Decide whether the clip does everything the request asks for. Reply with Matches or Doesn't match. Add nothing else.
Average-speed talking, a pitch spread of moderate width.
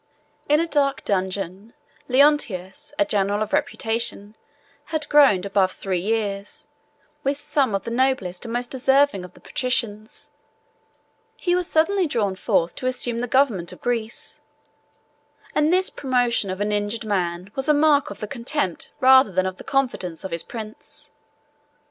Doesn't match